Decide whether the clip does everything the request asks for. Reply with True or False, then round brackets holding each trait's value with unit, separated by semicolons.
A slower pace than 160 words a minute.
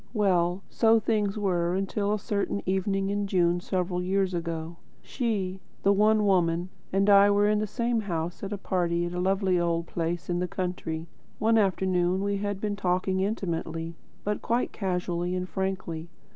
False (165 wpm)